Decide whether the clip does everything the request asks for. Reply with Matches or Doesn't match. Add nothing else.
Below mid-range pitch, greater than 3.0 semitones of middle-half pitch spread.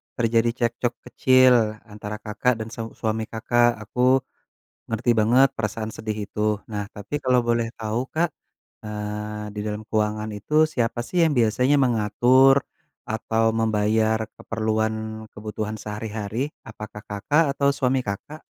Doesn't match